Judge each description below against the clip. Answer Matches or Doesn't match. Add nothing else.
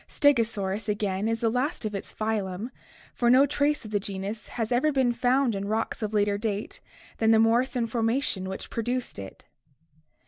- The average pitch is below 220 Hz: Doesn't match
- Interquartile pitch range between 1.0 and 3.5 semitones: Matches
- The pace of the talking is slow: Doesn't match